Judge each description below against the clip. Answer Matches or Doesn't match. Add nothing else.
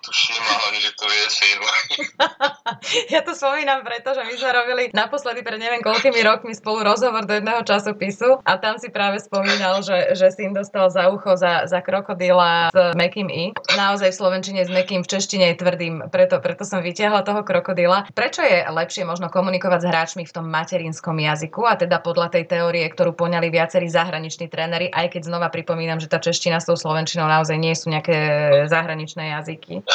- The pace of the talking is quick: Matches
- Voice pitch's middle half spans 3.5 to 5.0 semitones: Matches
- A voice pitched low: Doesn't match